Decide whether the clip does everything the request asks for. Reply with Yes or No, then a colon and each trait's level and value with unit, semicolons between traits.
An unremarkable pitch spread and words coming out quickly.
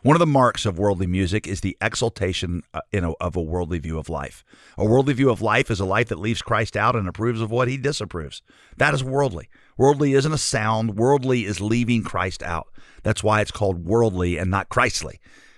Yes: average, 5.0 semitones; fast, 210 wpm